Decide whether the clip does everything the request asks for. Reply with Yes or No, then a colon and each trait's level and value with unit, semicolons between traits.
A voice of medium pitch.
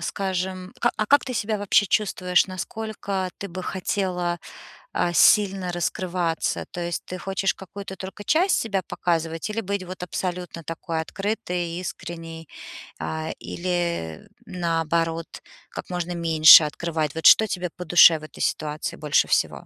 Yes: medium, 180 Hz